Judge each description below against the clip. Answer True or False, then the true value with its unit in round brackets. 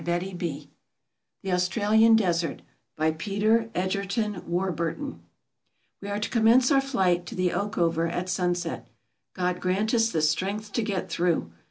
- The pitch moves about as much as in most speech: True (3.6 semitones)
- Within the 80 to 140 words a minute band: True (135 wpm)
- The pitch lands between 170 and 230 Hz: True (185 Hz)